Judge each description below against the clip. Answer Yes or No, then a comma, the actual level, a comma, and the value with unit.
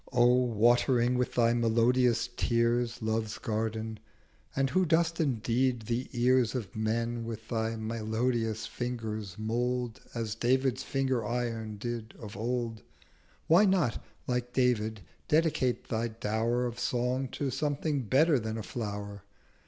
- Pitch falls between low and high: No, low, 120 Hz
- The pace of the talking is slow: Yes, slow, 130 wpm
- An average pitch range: No, narrow, 2.1 semitones